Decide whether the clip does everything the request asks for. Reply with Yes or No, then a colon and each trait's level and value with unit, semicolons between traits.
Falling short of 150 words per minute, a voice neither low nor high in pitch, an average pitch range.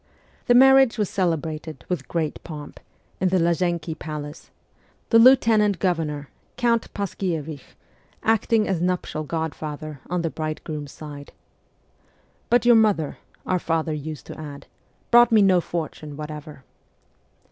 Yes: slow, 135 wpm; medium, 165 Hz; average, 4.8 semitones